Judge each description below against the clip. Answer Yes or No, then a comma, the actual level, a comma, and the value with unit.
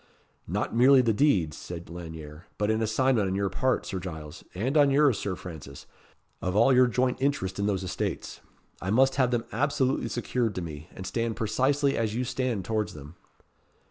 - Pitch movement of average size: No, wide, 5.9 semitones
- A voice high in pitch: No, low, 110 Hz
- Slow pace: No, average, 185 wpm